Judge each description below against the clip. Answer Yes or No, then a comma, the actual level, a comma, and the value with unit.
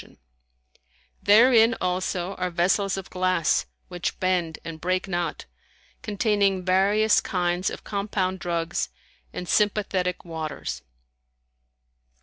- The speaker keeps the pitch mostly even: Yes, narrow, 2.3 semitones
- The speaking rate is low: Yes, slow, 105 wpm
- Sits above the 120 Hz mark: Yes, medium, 185 Hz